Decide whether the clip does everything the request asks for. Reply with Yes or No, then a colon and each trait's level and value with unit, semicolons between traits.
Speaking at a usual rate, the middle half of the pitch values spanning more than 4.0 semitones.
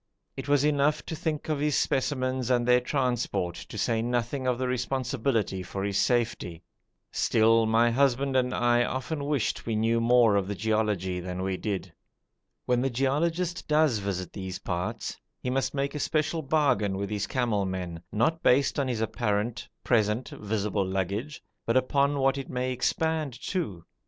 Yes: average, 165 wpm; average, 5.0 semitones